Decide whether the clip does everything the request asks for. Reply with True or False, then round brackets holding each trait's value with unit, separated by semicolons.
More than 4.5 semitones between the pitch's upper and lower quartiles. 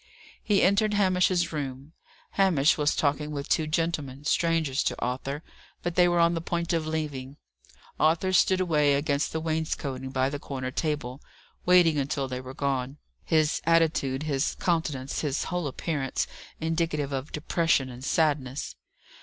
False (3.5 semitones)